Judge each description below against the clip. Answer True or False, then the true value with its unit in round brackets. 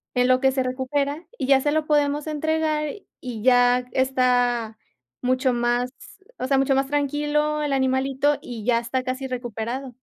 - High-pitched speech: True (265 Hz)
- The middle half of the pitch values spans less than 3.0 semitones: True (2.6 semitones)